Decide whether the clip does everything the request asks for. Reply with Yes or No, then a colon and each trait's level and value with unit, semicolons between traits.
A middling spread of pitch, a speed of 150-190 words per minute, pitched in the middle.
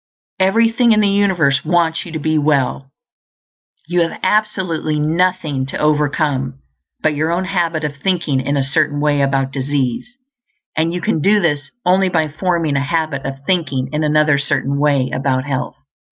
Yes: average, 3.9 semitones; average, 170 wpm; medium, 155 Hz